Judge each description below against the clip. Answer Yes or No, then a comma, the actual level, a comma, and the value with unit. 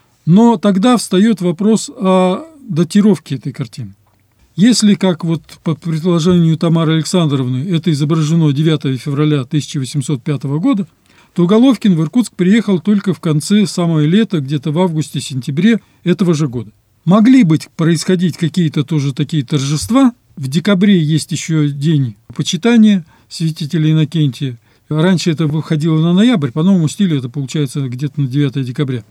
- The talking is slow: No, average, 135 wpm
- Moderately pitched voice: Yes, medium, 160 Hz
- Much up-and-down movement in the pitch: No, average, 4.2 semitones